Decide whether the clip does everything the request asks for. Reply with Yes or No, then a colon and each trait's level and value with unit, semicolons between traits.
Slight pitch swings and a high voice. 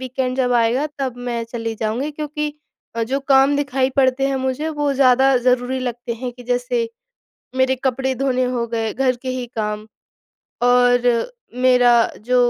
Yes: narrow, 1.7 semitones; very high, 255 Hz